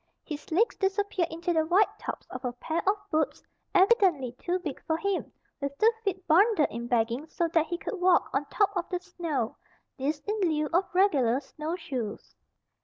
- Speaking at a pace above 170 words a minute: Yes, average, 180 wpm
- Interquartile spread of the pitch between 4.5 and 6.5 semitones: Yes, average, 4.8 semitones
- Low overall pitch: No, very high, 330 Hz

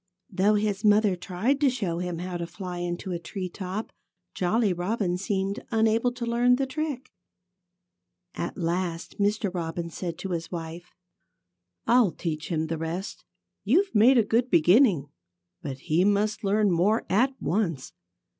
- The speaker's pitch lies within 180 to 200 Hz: Yes, high, 190 Hz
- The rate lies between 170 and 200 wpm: No, average, 155 wpm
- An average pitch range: Yes, average, 4.2 semitones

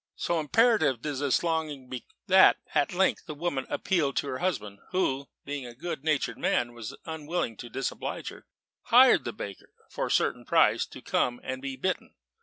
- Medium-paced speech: Yes, average, 185 wpm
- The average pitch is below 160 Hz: Yes, medium, 140 Hz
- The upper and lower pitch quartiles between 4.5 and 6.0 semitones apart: Yes, average, 4.8 semitones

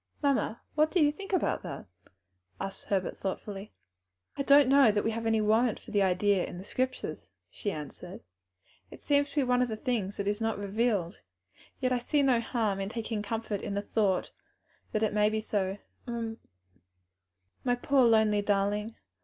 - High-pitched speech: Yes, high, 220 Hz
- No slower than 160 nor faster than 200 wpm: Yes, average, 180 wpm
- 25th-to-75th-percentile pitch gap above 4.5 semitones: No, average, 3.7 semitones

